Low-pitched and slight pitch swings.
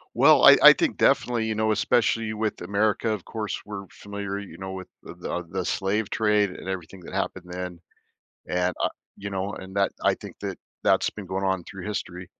Yes: low, 100 Hz; narrow, 2.1 semitones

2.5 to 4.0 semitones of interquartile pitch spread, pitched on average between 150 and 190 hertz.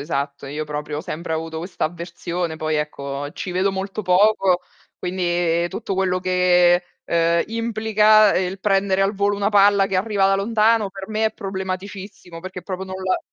Yes: average, 2.8 semitones; medium, 185 Hz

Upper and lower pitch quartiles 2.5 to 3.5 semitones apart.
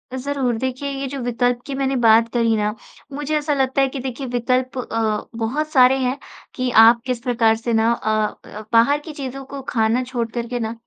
Yes: average, 2.9 semitones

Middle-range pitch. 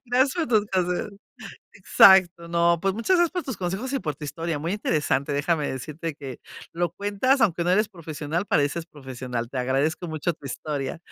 Yes: medium, 170 Hz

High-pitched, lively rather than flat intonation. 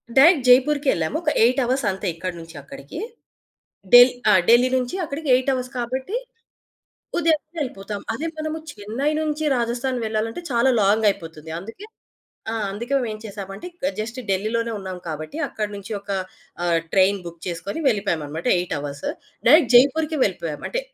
Yes: high, 230 Hz; wide, 5.7 semitones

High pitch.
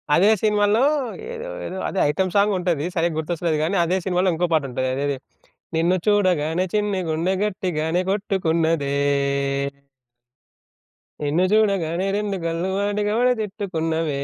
No: medium, 180 Hz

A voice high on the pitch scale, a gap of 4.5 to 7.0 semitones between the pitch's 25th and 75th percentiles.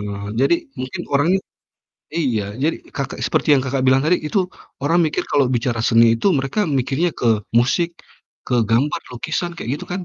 No: low, 135 Hz; average, 5.2 semitones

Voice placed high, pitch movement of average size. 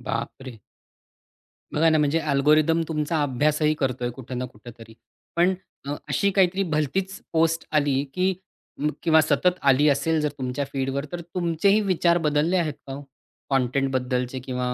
No: medium, 150 Hz; average, 3.9 semitones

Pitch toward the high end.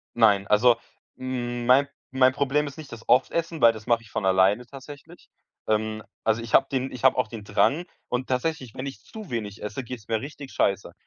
No: low, 125 Hz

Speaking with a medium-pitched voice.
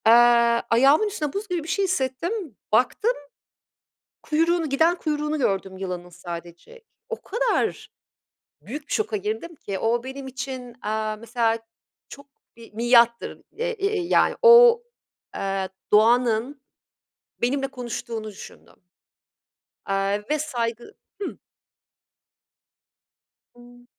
No: very high, 260 Hz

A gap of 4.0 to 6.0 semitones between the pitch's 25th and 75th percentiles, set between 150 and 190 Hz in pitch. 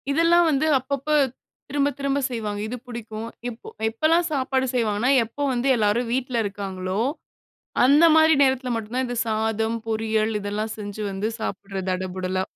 No: average, 4.4 semitones; high, 230 Hz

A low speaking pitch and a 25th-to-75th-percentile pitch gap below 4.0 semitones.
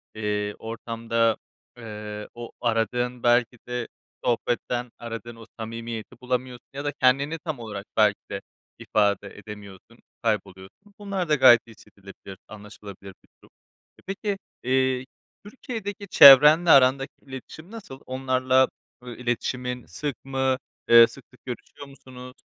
Yes: low, 125 Hz; average, 3.0 semitones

